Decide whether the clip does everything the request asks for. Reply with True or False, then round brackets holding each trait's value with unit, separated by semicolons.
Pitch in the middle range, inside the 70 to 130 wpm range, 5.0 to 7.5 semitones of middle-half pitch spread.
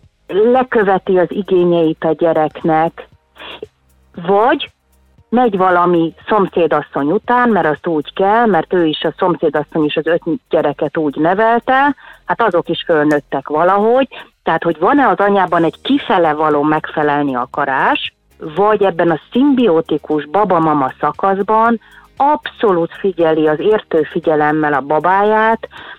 True (170 Hz; 120 wpm; 5.6 semitones)